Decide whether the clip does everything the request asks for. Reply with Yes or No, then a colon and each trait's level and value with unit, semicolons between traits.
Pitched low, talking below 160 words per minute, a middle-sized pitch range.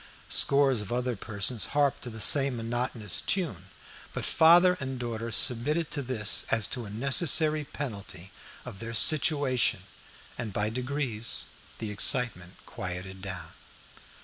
Yes: low, 120 Hz; slow, 135 wpm; average, 4.9 semitones